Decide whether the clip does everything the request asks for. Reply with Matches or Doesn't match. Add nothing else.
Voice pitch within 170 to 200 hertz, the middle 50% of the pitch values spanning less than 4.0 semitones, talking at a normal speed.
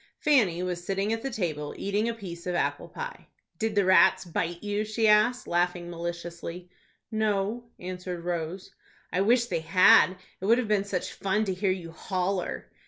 Matches